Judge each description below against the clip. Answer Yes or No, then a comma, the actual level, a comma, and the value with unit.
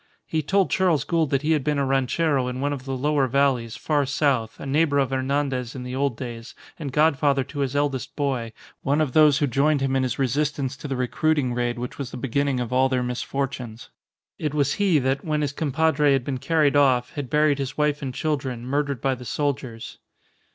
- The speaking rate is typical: No, fast, 215 wpm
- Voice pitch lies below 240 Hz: Yes, medium, 140 Hz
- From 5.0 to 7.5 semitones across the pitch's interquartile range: No, narrow, 2.5 semitones